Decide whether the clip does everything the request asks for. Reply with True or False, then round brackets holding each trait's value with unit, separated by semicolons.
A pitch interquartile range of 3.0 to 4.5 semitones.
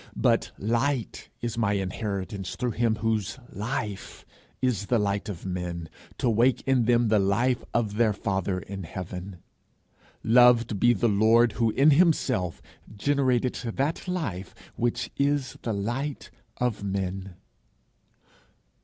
True (3.8 semitones)